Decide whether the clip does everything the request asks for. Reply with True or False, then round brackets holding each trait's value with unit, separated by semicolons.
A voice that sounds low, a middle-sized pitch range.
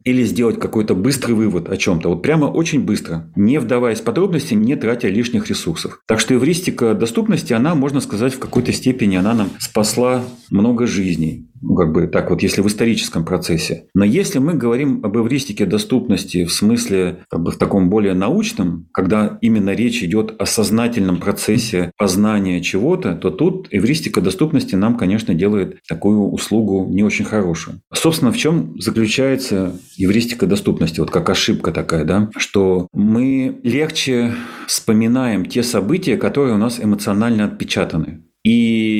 True (110 Hz; 4.5 semitones)